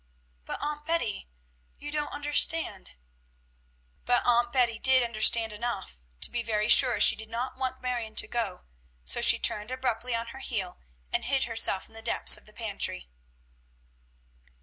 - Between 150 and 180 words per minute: Yes, average, 160 wpm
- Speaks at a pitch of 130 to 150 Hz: No, high, 235 Hz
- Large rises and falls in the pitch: No, average, 3.0 semitones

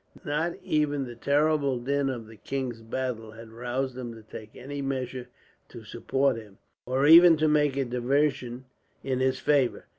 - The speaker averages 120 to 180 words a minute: Yes, average, 170 wpm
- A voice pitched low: Yes, low, 130 Hz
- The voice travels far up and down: No, average, 2.9 semitones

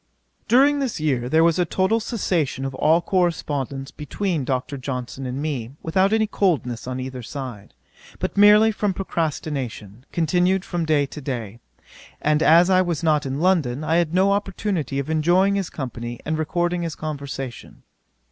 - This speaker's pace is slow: No, average, 165 wpm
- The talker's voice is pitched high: No, medium, 155 Hz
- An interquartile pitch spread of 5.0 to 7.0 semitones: Yes, wide, 5.5 semitones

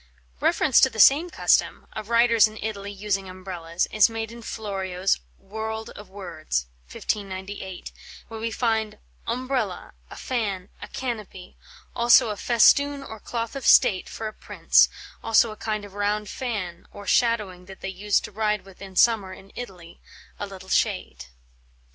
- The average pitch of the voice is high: Yes, high, 210 Hz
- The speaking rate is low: No, average, 160 wpm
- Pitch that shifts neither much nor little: Yes, average, 3.1 semitones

